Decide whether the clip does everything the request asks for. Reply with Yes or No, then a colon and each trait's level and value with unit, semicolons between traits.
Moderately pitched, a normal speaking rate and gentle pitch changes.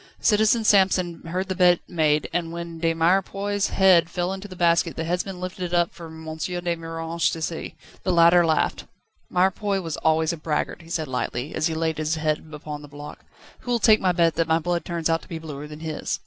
No: medium, 170 Hz; fast, 220 wpm; narrow, 2.2 semitones